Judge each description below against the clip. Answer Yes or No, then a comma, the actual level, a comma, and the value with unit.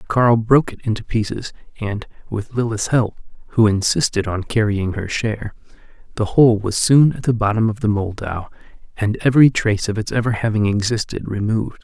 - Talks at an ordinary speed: Yes, average, 170 wpm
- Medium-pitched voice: No, low, 110 Hz